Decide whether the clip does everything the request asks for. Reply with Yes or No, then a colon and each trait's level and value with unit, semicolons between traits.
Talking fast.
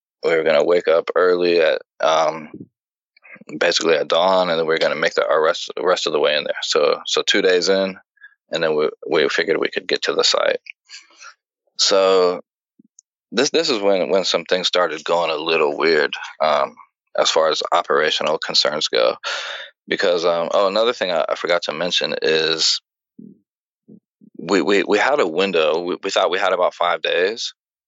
No: average, 185 wpm